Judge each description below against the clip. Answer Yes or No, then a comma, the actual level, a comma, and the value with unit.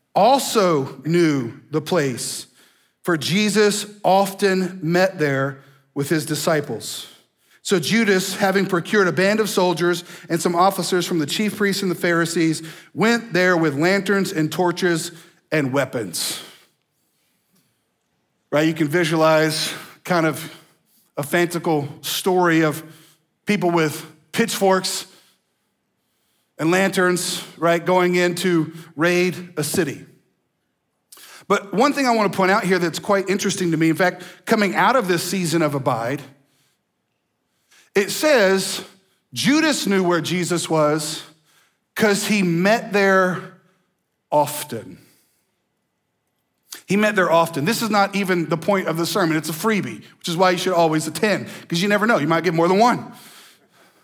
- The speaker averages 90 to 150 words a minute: Yes, average, 140 wpm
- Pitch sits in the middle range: Yes, medium, 175 Hz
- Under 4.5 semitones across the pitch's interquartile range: Yes, average, 3.3 semitones